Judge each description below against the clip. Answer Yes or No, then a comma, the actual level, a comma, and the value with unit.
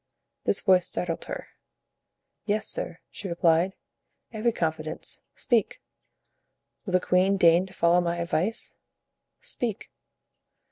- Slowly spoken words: Yes, slow, 110 wpm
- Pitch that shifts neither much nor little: Yes, average, 3.2 semitones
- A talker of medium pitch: Yes, medium, 180 Hz